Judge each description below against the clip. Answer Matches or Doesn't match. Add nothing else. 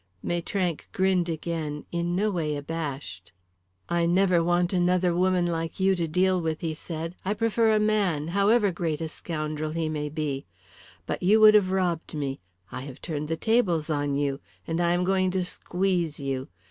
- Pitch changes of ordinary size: Matches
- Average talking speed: Matches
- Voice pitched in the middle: Matches